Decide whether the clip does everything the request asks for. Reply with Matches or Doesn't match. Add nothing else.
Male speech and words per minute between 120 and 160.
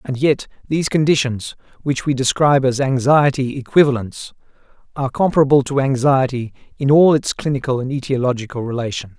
Matches